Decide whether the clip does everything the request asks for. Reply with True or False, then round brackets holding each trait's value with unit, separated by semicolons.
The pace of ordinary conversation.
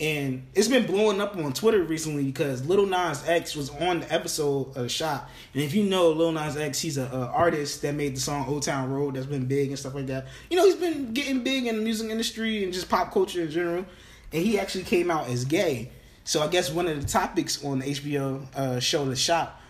False (240 wpm)